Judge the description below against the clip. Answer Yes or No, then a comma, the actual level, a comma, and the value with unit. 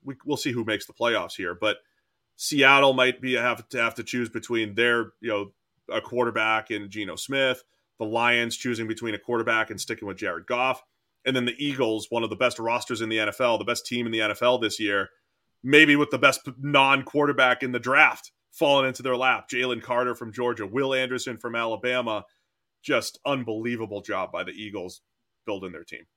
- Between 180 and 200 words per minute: Yes, average, 195 wpm